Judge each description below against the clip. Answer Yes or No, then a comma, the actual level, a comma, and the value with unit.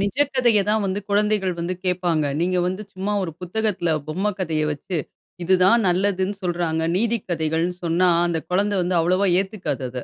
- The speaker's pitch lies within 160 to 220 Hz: Yes, medium, 185 Hz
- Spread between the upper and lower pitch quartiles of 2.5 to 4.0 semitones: Yes, average, 2.9 semitones